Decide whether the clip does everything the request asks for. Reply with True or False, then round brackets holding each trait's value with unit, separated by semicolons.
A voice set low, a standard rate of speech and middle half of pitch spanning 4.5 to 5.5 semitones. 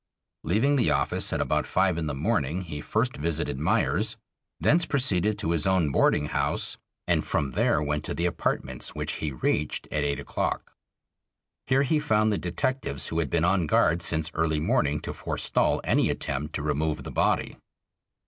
True (80 Hz; 175 wpm; 5.0 semitones)